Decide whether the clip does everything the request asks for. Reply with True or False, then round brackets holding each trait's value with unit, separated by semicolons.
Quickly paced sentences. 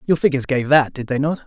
True (285 wpm)